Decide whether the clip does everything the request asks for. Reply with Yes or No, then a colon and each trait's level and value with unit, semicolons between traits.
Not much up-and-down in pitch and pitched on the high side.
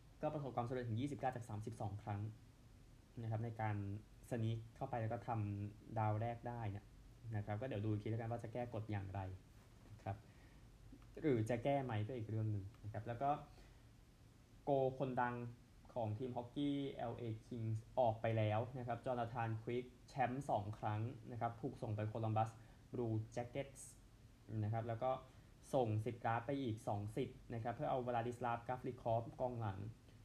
No: narrow, 2.3 semitones; low, 115 Hz